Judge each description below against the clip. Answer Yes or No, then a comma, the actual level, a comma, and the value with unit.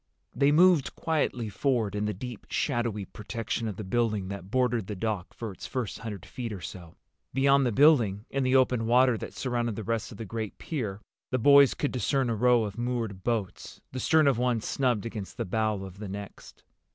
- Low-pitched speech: Yes, low, 115 Hz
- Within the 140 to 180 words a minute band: No, fast, 205 wpm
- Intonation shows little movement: No, average, 3.7 semitones